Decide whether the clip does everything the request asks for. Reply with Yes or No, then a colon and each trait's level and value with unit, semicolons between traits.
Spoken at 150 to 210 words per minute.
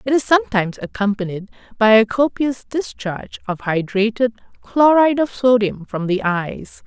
No: average, 140 wpm